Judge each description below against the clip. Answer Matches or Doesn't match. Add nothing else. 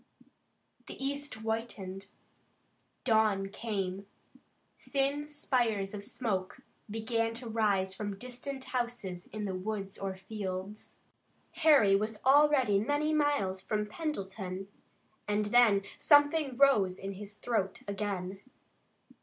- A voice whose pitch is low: Doesn't match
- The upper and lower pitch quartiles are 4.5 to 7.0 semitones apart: Matches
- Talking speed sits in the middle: Doesn't match